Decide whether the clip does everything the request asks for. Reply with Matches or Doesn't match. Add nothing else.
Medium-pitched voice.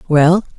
Matches